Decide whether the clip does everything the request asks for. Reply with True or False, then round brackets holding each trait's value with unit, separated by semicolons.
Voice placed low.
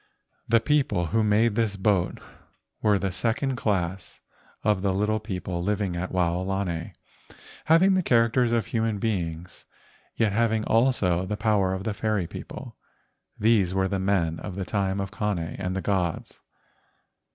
True (100 Hz)